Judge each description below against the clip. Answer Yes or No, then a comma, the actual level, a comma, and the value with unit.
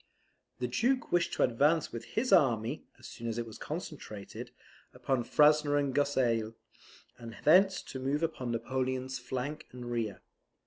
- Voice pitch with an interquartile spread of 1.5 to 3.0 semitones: No, average, 4.2 semitones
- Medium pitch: No, low, 130 Hz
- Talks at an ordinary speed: Yes, average, 150 wpm